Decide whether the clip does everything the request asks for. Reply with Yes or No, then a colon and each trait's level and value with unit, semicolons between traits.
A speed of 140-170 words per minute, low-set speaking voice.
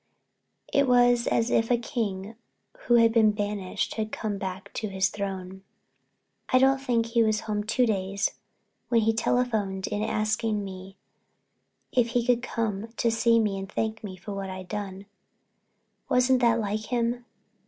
No: average, 165 wpm; high, 220 Hz